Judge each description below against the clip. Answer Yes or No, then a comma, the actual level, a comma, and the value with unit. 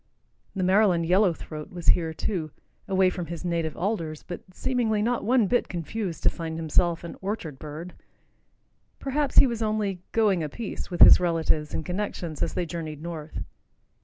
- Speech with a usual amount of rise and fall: Yes, average, 4.3 semitones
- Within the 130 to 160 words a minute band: No, average, 170 wpm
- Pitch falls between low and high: Yes, medium, 180 Hz